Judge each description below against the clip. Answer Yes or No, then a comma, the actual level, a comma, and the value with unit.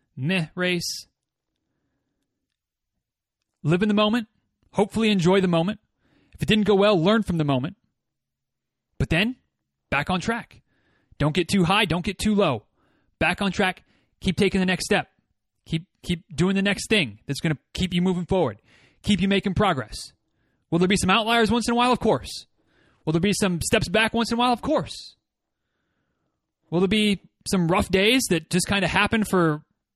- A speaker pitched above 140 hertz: Yes, medium, 185 Hz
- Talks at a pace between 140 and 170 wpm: No, average, 180 wpm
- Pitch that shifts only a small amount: No, average, 4.4 semitones